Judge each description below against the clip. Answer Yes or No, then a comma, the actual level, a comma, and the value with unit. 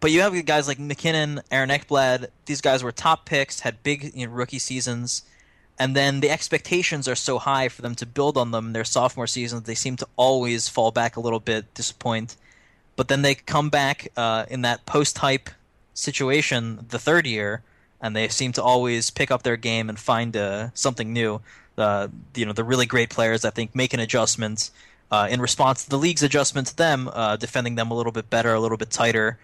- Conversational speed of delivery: No, fast, 215 wpm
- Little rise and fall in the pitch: No, average, 3.3 semitones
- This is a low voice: Yes, low, 125 Hz